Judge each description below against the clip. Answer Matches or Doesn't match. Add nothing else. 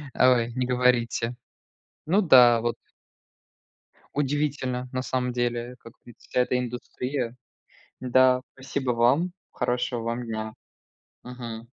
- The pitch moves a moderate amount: Doesn't match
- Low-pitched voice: Matches